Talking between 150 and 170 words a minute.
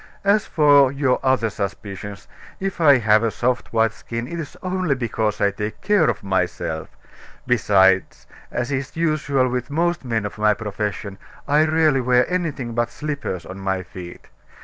Yes: average, 165 wpm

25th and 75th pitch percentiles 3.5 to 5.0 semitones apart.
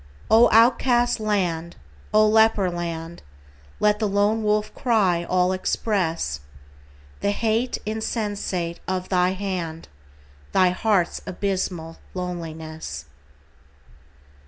Yes: average, 3.9 semitones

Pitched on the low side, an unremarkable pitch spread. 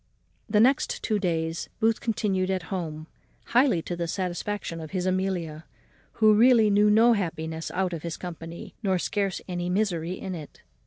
No: medium, 185 Hz; average, 3.9 semitones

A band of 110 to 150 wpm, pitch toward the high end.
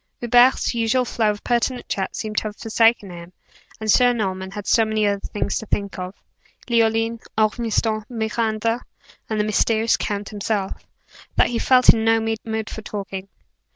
No: average, 165 wpm; high, 220 Hz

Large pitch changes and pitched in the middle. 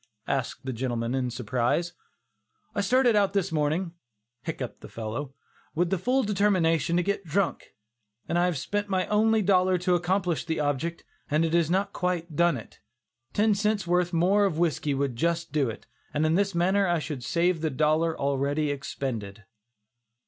No: average, 4.8 semitones; medium, 170 Hz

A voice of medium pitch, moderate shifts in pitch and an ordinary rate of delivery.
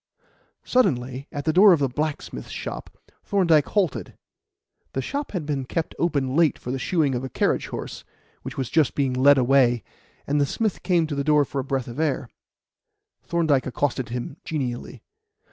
Yes: medium, 145 Hz; average, 3.7 semitones; average, 180 wpm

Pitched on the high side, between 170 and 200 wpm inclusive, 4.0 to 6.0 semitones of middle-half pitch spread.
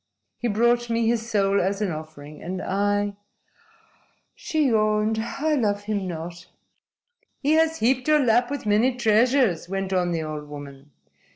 No: high, 210 Hz; average, 155 wpm; average, 4.7 semitones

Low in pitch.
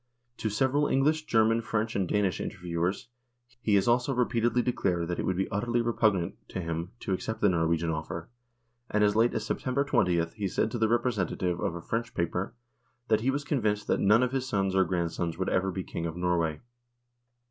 Yes: low, 100 Hz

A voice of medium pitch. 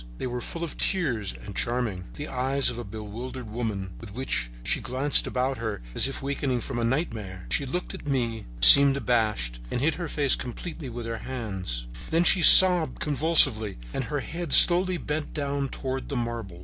No: low, 130 Hz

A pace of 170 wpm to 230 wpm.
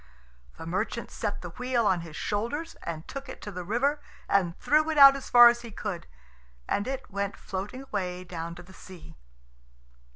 Yes: average, 190 wpm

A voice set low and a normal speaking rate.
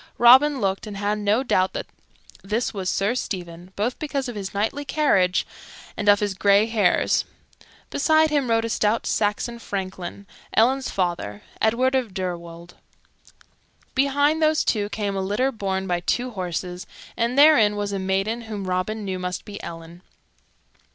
No: high, 205 Hz; average, 160 wpm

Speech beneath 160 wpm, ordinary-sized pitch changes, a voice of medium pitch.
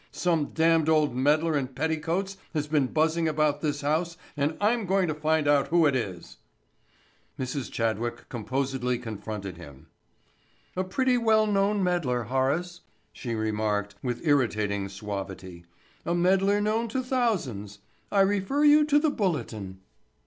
No: average, 140 wpm; wide, 7.7 semitones; medium, 150 Hz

